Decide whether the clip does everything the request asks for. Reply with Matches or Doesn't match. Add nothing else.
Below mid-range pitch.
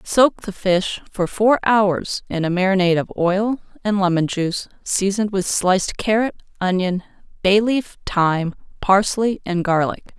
Doesn't match